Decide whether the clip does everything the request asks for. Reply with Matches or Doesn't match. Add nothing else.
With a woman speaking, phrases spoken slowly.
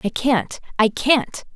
Matches